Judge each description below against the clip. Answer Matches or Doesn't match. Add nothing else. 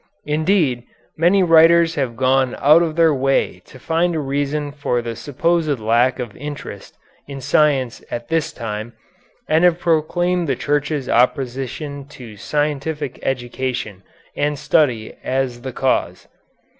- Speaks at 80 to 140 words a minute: Matches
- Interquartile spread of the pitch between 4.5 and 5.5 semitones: Doesn't match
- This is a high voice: Doesn't match